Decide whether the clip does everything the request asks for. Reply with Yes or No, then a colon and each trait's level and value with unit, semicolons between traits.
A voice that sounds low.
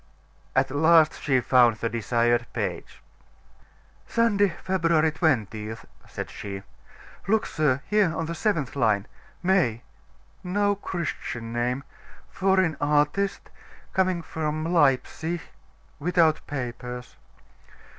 No: medium, 155 Hz